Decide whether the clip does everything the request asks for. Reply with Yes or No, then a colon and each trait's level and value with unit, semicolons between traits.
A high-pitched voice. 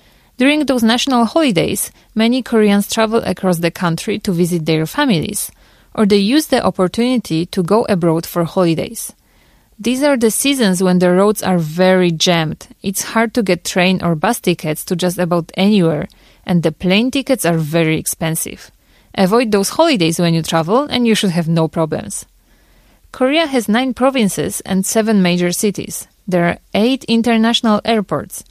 Yes: high, 195 Hz